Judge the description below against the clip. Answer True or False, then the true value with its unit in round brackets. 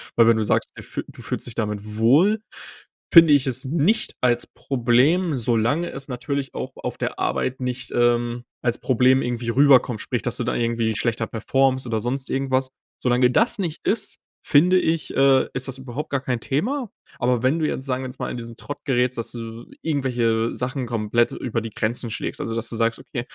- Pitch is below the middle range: True (125 Hz)